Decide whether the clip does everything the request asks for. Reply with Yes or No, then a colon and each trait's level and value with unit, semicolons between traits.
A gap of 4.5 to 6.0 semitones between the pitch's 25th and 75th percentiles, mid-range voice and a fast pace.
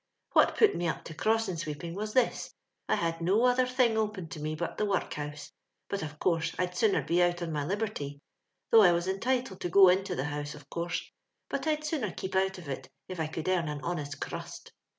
Yes: average, 4.8 semitones; medium, 180 Hz; fast, 230 wpm